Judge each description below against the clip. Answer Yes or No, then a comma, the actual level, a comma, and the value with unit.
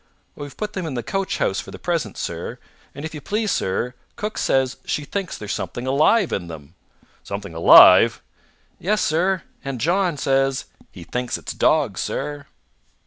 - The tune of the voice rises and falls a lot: Yes, wide, 7.0 semitones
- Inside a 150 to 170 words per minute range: Yes, average, 165 wpm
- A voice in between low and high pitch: Yes, medium, 145 Hz